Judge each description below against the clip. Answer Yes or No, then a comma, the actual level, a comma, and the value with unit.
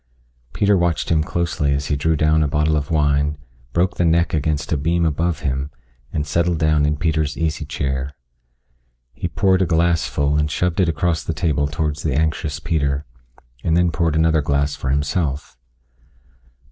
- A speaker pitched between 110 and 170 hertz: No, very low, 75 Hz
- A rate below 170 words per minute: No, average, 175 wpm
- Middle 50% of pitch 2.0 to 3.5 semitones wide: Yes, narrow, 2.4 semitones